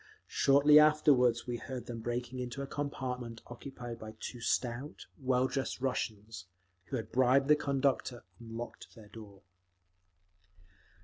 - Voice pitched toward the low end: Yes, low, 125 Hz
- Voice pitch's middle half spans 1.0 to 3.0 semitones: Yes, average, 2.7 semitones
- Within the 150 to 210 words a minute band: No, slow, 135 wpm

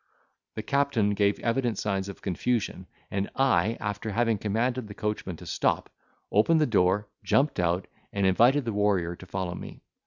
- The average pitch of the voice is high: No, low, 105 Hz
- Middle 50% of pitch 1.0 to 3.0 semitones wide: No, average, 3.6 semitones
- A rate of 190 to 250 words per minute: No, average, 165 wpm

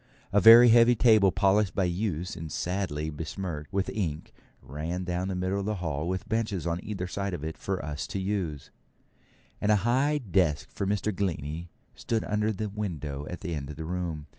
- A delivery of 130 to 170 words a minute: No, average, 195 wpm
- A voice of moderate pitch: No, very low, 95 Hz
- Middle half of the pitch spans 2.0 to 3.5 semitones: No, average, 4.5 semitones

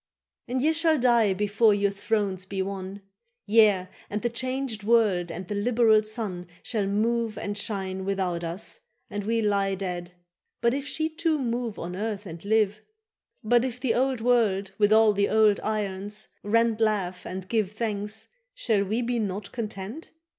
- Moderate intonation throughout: Yes, average, 3.0 semitones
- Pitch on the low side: No, high, 210 Hz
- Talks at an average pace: Yes, average, 170 wpm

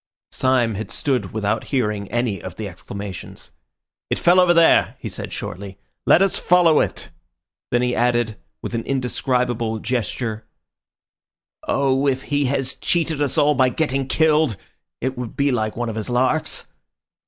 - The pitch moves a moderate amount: Yes, average, 4.1 semitones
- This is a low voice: Yes, low, 125 Hz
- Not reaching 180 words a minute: Yes, average, 155 wpm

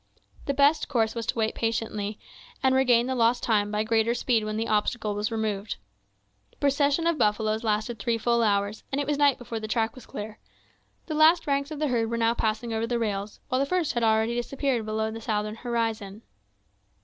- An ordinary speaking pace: No, fast, 210 wpm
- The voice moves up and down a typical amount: Yes, average, 3.0 semitones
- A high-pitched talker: Yes, high, 230 Hz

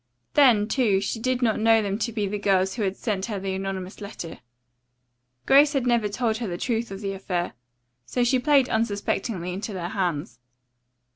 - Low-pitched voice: No, high, 210 Hz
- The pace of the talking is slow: No, average, 190 wpm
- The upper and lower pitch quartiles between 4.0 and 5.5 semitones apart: No, average, 3.6 semitones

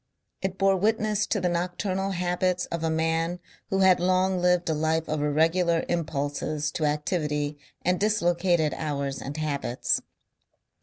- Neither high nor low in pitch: Yes, medium, 170 Hz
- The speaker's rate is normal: Yes, average, 145 wpm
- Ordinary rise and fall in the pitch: Yes, average, 3.2 semitones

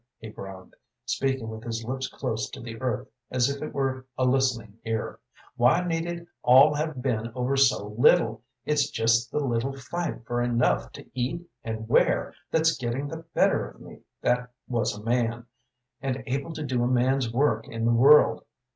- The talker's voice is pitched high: No, low, 125 Hz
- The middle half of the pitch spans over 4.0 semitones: No, average, 3.1 semitones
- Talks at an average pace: Yes, average, 180 wpm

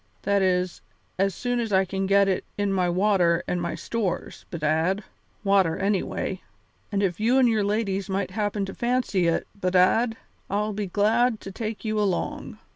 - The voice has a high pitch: Yes, high, 195 Hz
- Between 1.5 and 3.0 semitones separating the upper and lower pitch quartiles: Yes, narrow, 2.4 semitones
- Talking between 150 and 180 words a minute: Yes, average, 170 wpm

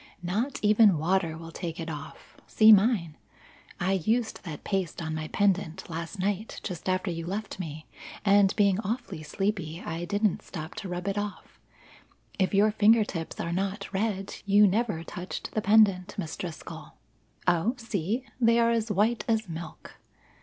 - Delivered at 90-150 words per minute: No, average, 165 wpm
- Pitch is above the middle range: Yes, high, 195 Hz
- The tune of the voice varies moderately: Yes, average, 4.0 semitones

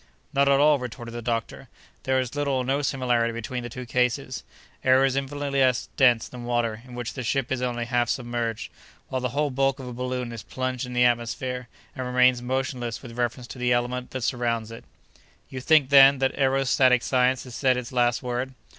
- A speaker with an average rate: No, fast, 210 wpm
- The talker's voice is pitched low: Yes, low, 125 Hz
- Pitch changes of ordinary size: No, narrow, 1.6 semitones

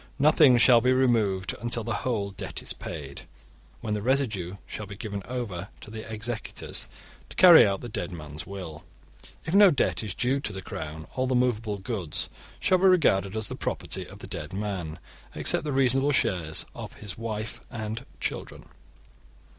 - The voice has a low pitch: Yes, low, 110 Hz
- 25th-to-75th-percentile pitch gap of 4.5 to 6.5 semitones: Yes, average, 4.8 semitones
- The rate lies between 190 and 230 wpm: No, average, 180 wpm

